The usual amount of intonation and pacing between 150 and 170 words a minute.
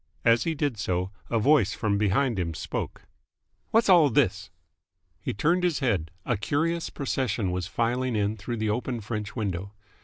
No: wide, 5.8 semitones; average, 160 wpm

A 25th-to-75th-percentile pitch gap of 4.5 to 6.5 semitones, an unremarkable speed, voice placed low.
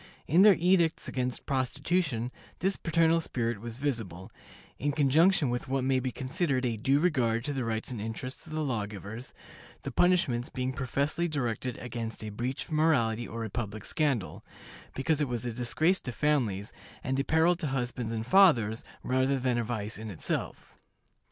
Yes: average, 4.8 semitones; average, 175 wpm; low, 130 Hz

